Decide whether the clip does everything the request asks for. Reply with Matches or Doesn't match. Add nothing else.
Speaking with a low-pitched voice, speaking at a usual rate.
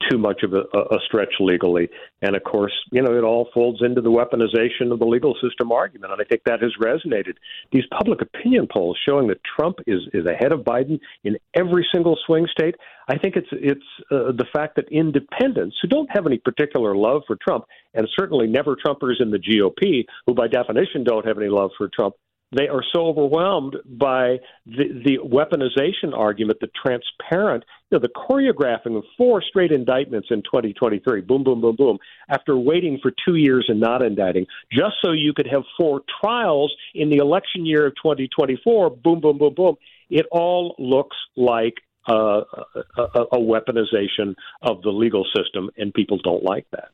Matches